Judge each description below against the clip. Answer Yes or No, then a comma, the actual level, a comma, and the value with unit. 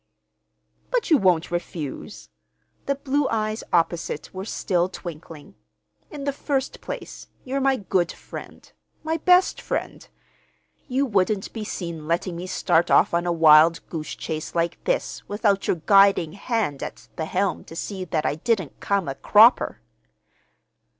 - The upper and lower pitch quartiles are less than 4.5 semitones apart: No, wide, 5.6 semitones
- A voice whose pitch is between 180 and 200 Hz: Yes, high, 190 Hz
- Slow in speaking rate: No, average, 145 wpm